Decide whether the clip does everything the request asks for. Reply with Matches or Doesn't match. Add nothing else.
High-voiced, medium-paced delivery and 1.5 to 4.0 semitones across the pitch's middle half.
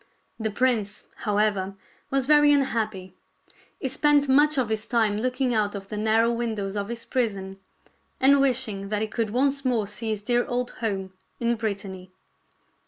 Matches